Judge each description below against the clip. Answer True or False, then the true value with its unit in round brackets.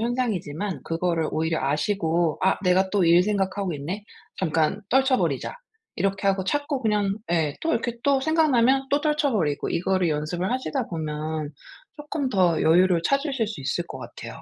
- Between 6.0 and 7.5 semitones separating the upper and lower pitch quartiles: True (7.0 semitones)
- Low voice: False (190 Hz)